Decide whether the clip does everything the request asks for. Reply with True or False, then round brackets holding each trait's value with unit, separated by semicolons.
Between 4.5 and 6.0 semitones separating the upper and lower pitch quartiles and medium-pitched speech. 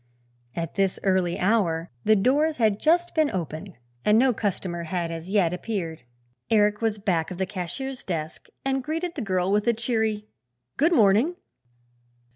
False (5.1 semitones; 205 Hz)